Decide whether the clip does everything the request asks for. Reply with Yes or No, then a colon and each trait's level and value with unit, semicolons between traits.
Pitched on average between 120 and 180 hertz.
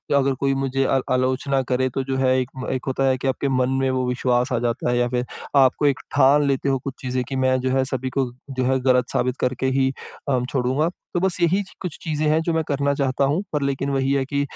Yes: low, 135 Hz